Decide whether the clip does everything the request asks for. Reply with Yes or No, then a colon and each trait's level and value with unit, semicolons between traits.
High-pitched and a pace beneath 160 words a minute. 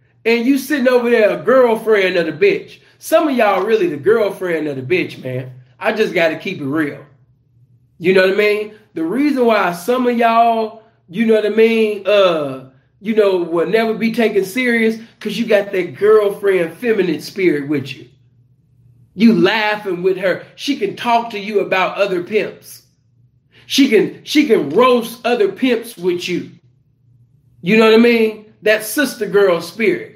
No: high, 205 Hz; average, 175 wpm